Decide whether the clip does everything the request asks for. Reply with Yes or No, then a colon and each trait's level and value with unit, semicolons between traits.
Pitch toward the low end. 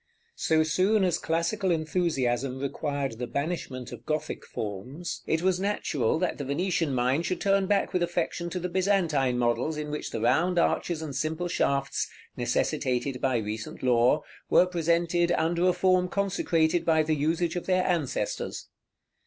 No: medium, 160 Hz